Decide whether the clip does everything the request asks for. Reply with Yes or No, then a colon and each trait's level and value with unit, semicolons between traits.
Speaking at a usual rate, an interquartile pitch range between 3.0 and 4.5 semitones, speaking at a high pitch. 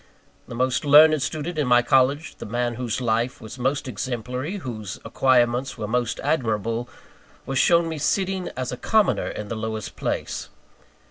No: average, 160 wpm; average, 3.9 semitones; low, 125 Hz